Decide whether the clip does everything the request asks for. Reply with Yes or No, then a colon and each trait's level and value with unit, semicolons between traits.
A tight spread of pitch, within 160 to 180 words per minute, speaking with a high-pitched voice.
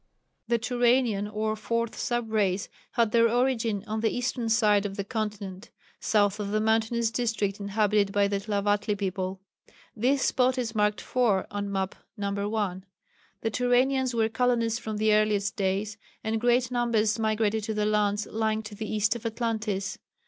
Yes: narrow, 2.2 semitones; average, 165 wpm; high, 215 Hz